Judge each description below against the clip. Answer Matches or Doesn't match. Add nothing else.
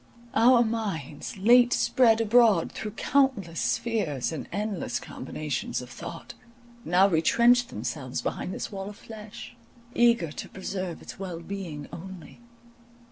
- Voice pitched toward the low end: Doesn't match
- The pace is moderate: Doesn't match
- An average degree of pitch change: Doesn't match